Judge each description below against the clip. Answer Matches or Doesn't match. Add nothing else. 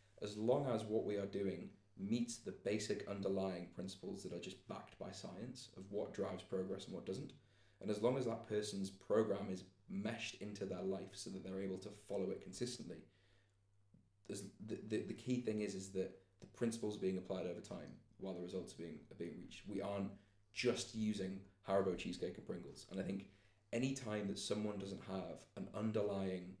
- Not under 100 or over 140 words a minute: Doesn't match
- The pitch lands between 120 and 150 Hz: Doesn't match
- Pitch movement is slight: Matches